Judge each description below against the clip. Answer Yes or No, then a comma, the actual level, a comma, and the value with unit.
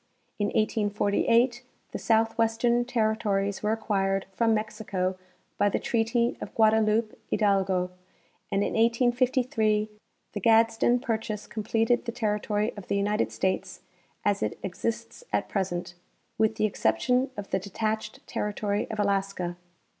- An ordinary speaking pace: No, slow, 125 wpm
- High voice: Yes, high, 215 Hz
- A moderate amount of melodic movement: No, narrow, 2.1 semitones